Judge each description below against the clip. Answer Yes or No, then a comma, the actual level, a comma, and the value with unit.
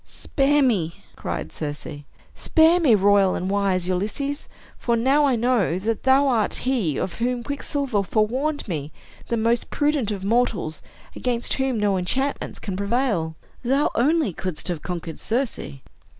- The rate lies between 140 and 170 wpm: Yes, average, 150 wpm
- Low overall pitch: No, high, 230 Hz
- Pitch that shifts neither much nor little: No, wide, 6.2 semitones